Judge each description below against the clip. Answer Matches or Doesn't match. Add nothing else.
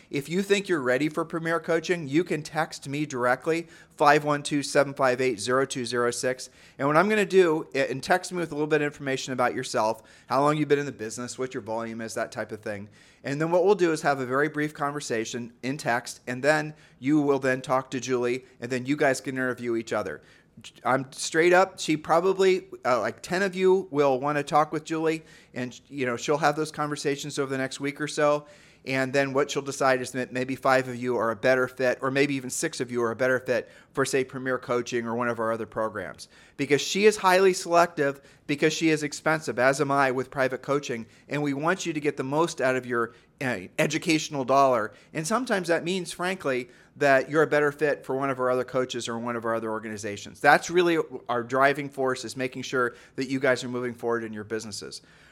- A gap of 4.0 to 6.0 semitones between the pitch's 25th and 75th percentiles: Doesn't match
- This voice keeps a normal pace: Doesn't match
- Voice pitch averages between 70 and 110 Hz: Doesn't match